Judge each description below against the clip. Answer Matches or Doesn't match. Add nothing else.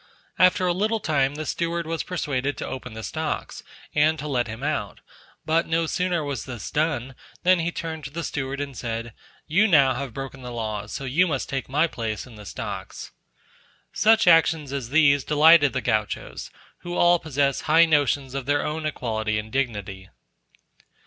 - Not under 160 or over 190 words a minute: Matches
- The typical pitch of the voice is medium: Matches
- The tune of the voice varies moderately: Matches